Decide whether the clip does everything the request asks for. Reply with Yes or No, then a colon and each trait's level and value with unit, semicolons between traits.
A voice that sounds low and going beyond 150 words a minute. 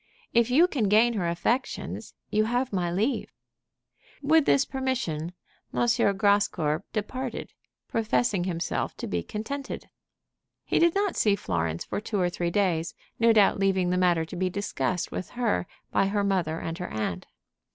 No: high, 200 Hz; average, 160 wpm